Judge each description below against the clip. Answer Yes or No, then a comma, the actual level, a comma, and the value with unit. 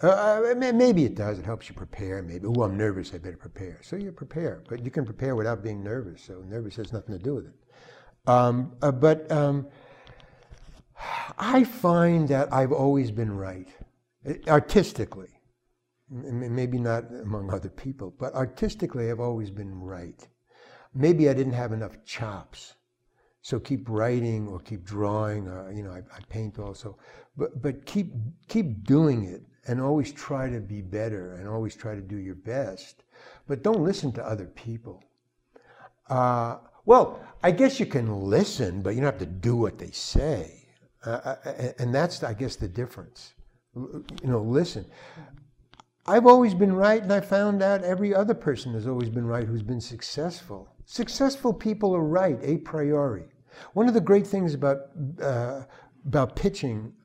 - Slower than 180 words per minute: Yes, average, 165 wpm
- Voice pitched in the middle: No, low, 125 Hz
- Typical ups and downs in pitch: No, wide, 6.0 semitones